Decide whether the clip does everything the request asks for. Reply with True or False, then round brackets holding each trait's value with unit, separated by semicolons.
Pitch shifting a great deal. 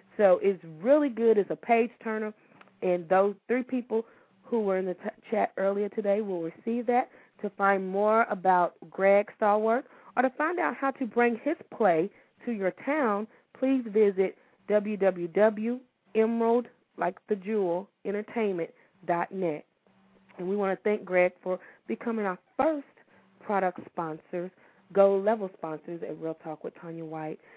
False (3.8 semitones)